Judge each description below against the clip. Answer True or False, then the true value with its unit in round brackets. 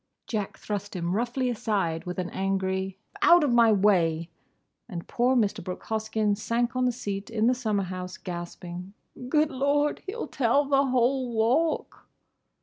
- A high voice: True (220 Hz)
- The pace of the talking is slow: False (155 wpm)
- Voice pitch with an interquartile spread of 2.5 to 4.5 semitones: False (4.9 semitones)